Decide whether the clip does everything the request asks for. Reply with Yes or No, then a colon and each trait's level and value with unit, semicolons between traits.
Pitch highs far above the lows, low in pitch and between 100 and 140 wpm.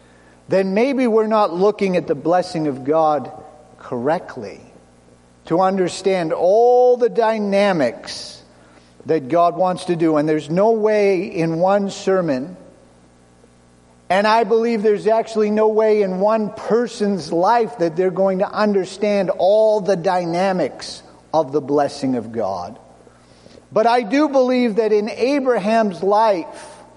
No: wide, 6.1 semitones; high, 190 Hz; slow, 135 wpm